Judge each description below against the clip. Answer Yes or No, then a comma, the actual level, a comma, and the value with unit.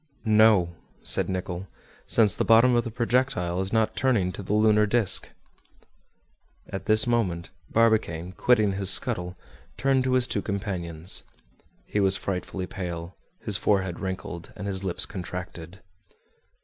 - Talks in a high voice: No, low, 100 Hz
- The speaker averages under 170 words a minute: Yes, average, 140 wpm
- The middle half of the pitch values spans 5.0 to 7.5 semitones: No, average, 3.4 semitones